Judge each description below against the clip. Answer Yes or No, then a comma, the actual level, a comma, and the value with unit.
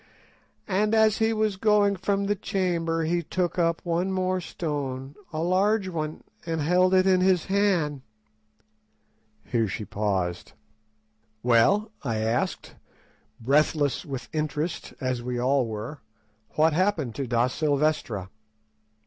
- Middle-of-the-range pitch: Yes, medium, 160 Hz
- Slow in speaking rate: Yes, slow, 130 wpm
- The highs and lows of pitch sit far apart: Yes, wide, 6.3 semitones